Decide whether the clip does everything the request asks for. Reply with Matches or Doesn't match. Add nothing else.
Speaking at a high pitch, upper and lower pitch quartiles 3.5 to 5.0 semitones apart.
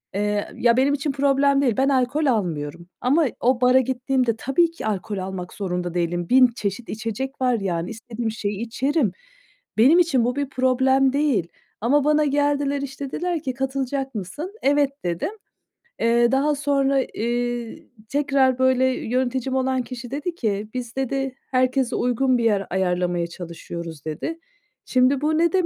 Matches